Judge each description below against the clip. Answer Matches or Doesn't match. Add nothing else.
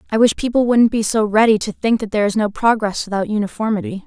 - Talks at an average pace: Doesn't match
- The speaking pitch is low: Doesn't match